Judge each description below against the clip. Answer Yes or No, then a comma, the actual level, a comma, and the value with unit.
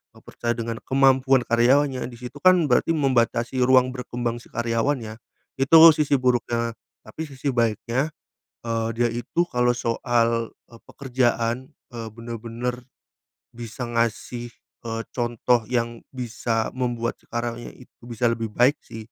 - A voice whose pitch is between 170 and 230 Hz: No, low, 120 Hz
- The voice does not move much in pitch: Yes, narrow, 1.6 semitones